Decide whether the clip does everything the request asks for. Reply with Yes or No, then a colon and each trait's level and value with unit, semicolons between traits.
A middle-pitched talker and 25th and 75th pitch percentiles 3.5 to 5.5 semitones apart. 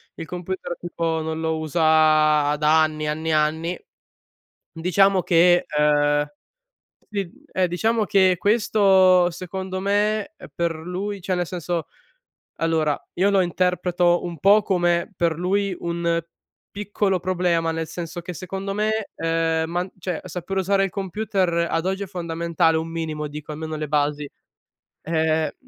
No: medium, 175 Hz; average, 2.8 semitones